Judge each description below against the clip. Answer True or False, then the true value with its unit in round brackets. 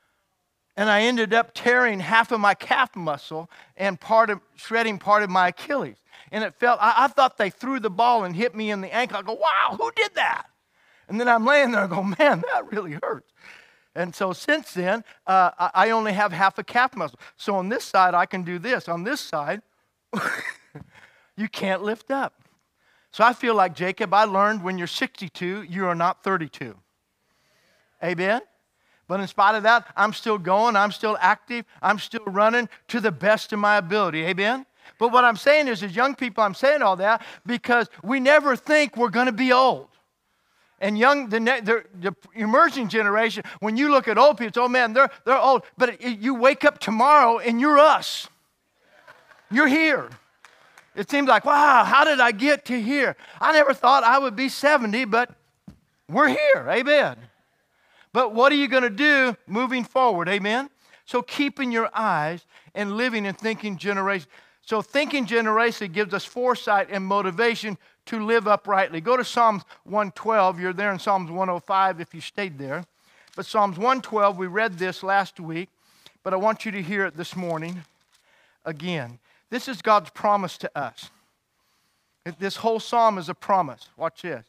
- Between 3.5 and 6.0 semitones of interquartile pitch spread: True (4.5 semitones)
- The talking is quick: False (185 wpm)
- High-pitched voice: True (220 Hz)